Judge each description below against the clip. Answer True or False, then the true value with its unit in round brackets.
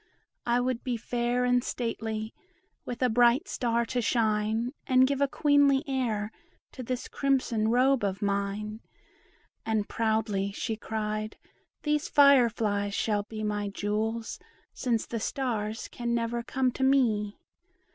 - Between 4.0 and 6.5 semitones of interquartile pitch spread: False (2.9 semitones)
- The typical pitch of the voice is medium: False (230 Hz)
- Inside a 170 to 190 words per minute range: False (140 wpm)